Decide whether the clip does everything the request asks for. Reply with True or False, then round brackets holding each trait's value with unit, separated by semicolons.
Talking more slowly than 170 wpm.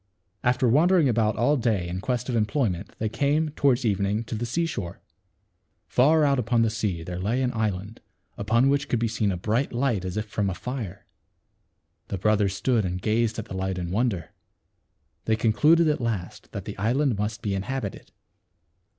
False (185 wpm)